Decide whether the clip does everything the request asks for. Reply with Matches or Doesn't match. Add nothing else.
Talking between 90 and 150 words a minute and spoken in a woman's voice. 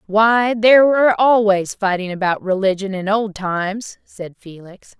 Matches